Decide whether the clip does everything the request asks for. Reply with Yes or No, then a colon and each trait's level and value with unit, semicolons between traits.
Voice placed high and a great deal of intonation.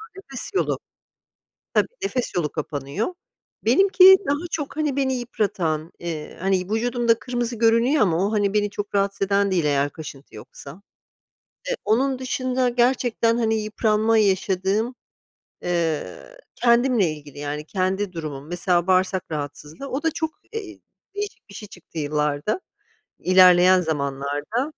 Yes: high, 200 Hz; wide, 7.1 semitones